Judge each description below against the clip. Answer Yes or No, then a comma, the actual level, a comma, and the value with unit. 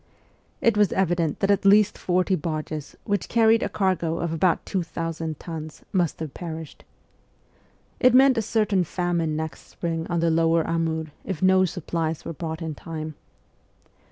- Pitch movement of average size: Yes, average, 3.0 semitones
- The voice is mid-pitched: Yes, medium, 170 Hz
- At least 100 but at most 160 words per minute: Yes, average, 155 wpm